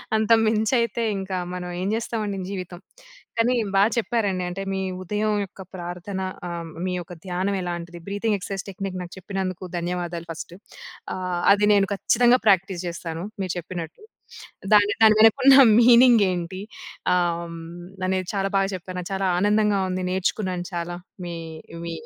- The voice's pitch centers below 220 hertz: Yes, high, 190 Hz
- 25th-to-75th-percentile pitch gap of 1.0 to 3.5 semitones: Yes, average, 2.9 semitones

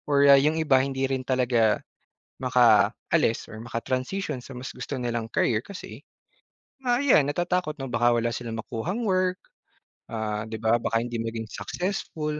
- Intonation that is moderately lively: Yes, average, 4.7 semitones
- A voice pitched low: Yes, low, 125 Hz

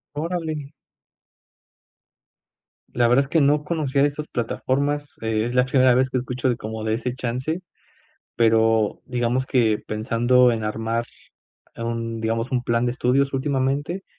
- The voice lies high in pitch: No, low, 125 Hz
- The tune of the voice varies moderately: Yes, average, 3.2 semitones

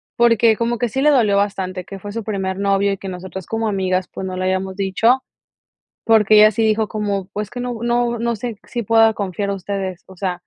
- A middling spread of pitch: Yes, average, 3.0 semitones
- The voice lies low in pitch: No, high, 205 Hz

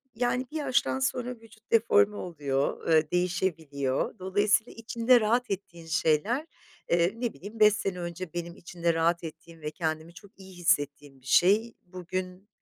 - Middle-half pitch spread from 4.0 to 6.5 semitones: Yes, average, 4.8 semitones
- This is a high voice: No, medium, 180 Hz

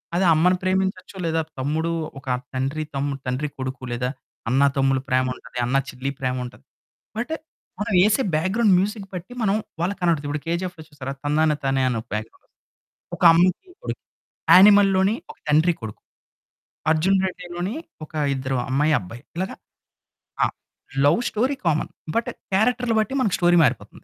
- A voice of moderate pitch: Yes, medium, 160 Hz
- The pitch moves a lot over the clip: Yes, wide, 5.9 semitones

